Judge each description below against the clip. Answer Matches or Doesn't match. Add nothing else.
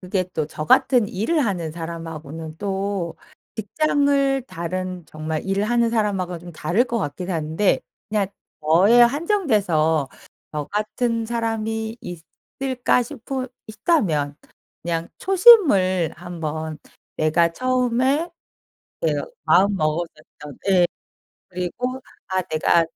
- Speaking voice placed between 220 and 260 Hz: Doesn't match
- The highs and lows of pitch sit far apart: Matches